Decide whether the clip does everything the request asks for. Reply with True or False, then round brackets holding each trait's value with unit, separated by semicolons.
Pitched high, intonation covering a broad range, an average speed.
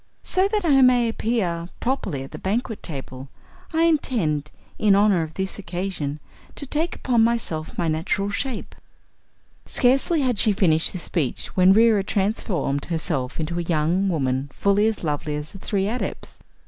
True (195 Hz; 6.6 semitones; 160 wpm)